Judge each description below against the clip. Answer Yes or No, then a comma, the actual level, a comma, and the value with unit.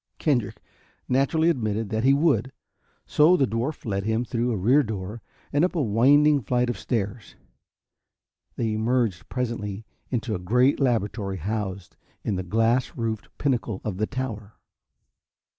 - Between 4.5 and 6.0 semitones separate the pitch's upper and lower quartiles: No, average, 3.7 semitones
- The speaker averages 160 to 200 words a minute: No, average, 145 wpm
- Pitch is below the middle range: Yes, low, 115 Hz